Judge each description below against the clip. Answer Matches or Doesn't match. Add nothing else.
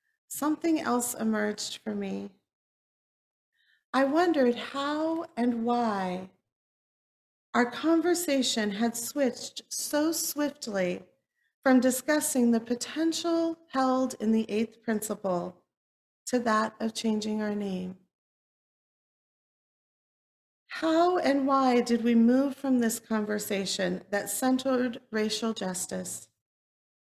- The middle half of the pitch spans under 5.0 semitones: Matches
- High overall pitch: Matches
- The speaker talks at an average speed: Doesn't match